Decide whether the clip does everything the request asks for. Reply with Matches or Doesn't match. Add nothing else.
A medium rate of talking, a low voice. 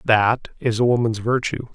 Matches